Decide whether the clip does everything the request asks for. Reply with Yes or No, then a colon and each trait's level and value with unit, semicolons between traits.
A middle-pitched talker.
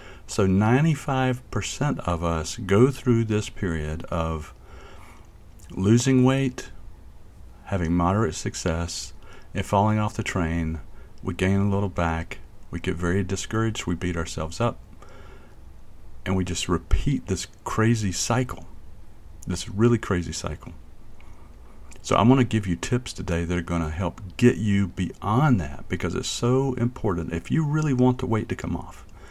No: very low, 95 Hz